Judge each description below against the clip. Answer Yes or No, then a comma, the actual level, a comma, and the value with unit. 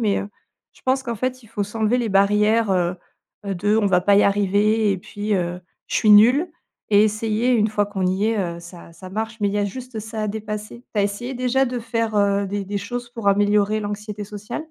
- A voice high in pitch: Yes, high, 210 Hz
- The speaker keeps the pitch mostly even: Yes, narrow, 2.0 semitones